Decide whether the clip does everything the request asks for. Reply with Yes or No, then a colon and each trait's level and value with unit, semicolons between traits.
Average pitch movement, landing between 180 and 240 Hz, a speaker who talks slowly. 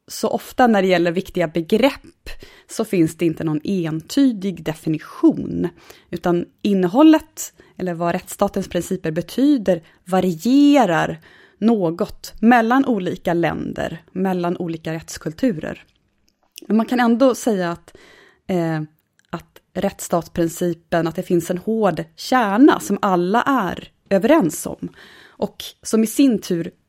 No: wide, 5.7 semitones; medium, 185 Hz; slow, 120 wpm